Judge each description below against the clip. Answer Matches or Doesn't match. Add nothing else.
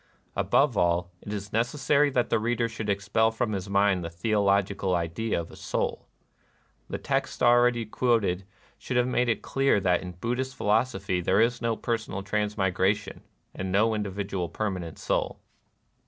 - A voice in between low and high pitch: Doesn't match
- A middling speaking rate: Matches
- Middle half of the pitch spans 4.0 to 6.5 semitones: Doesn't match